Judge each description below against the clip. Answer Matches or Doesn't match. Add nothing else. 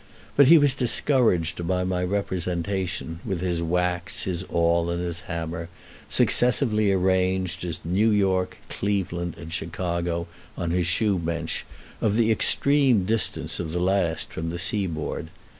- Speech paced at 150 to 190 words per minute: Doesn't match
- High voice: Doesn't match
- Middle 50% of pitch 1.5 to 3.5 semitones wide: Matches